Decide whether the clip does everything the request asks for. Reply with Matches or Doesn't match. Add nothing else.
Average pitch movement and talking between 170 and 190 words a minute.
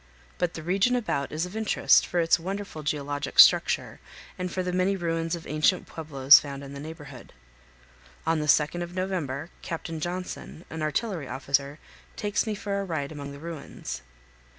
Matches